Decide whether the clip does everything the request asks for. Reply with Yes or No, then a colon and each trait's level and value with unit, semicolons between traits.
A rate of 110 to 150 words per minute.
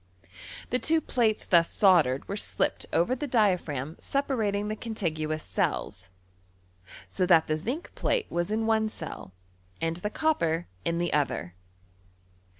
Yes: average, 140 wpm